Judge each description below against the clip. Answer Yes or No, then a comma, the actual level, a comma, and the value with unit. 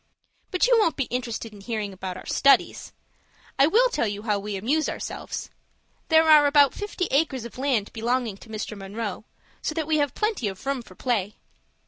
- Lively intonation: Yes, wide, 6.4 semitones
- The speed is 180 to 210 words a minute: Yes, average, 190 wpm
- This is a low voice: No, high, 245 Hz